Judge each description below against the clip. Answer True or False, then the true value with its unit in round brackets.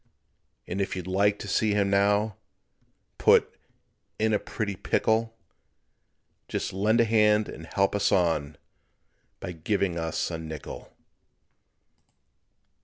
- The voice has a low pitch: True (100 Hz)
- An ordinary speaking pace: False (120 wpm)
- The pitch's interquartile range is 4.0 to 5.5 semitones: False (3.3 semitones)